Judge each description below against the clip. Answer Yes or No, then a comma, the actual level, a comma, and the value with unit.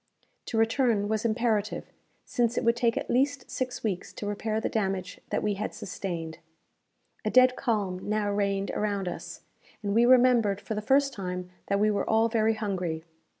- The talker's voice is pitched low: No, high, 215 Hz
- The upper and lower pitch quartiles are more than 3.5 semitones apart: No, average, 2.9 semitones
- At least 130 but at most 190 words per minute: Yes, average, 180 wpm